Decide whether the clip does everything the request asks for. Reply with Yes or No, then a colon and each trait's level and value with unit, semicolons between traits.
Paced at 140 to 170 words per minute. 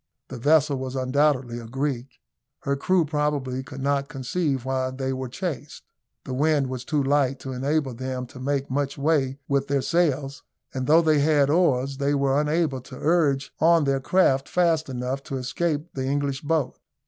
No: average, 180 wpm